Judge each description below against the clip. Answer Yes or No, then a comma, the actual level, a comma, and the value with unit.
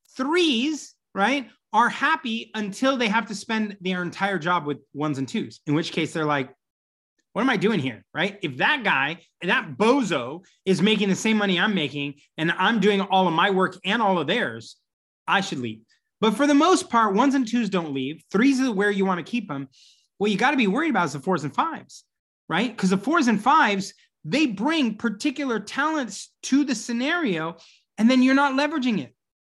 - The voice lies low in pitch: No, high, 205 Hz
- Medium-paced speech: No, fast, 210 wpm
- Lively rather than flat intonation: Yes, wide, 7.1 semitones